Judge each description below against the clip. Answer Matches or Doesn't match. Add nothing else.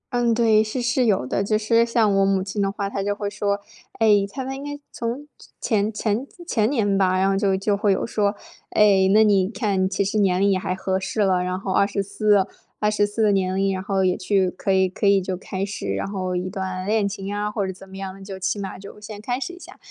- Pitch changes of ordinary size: Doesn't match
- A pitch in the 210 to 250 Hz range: Doesn't match